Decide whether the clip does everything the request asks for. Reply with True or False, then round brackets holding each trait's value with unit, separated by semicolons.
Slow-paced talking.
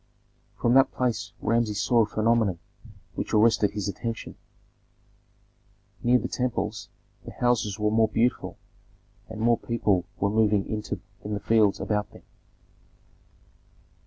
True (125 wpm)